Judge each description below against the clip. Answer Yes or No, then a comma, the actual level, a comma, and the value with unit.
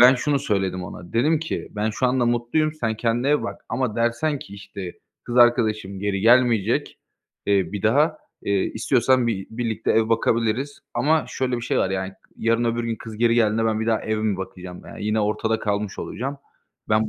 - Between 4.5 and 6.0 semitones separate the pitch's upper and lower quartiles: No, average, 2.8 semitones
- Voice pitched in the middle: No, low, 115 Hz